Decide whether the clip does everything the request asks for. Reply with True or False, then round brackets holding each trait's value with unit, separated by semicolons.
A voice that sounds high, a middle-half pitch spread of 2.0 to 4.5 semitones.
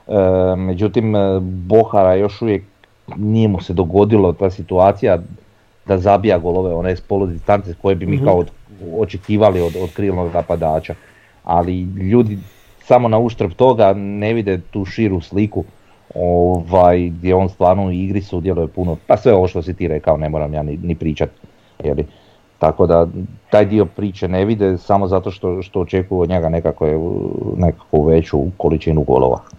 False (95 Hz; 2.7 semitones)